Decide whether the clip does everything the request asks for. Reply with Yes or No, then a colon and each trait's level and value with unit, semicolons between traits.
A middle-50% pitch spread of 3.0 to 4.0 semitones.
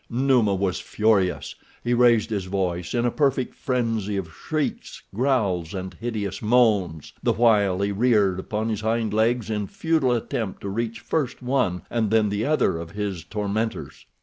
Yes: average, 3.6 semitones